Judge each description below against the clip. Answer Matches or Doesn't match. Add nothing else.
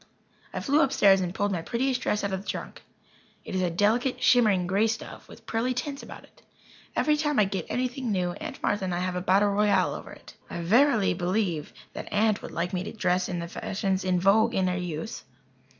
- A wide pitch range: Doesn't match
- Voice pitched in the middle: Doesn't match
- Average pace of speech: Doesn't match